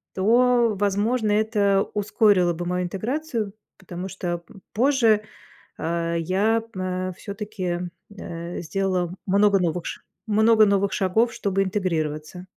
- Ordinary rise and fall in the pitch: Yes, average, 3.2 semitones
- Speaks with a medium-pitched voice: No, high, 195 Hz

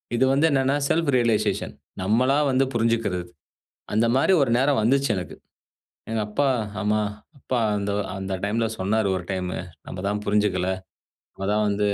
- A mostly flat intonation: No, average, 4.5 semitones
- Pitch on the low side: Yes, low, 110 Hz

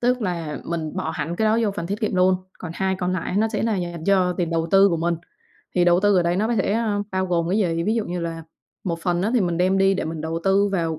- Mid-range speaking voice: Yes, medium, 180 Hz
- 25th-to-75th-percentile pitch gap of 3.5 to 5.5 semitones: No, average, 2.9 semitones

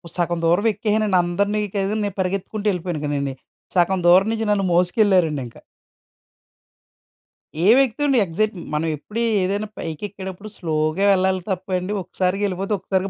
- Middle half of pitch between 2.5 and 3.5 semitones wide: Yes, average, 2.9 semitones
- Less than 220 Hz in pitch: Yes, high, 190 Hz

